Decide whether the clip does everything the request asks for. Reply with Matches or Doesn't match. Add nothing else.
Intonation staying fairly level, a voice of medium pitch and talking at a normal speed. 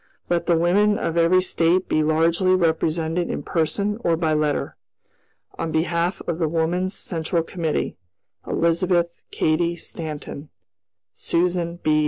Doesn't match